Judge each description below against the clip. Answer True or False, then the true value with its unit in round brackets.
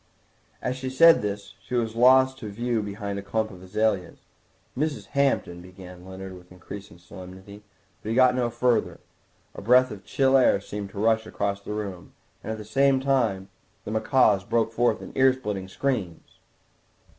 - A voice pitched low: True (110 Hz)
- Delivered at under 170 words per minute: False (175 wpm)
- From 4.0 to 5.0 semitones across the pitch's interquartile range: True (4.5 semitones)